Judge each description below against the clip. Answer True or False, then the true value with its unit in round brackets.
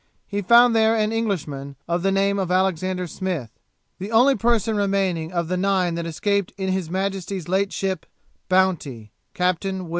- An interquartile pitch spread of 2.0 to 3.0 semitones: True (2.5 semitones)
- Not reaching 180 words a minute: True (160 wpm)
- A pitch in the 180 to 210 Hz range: True (190 Hz)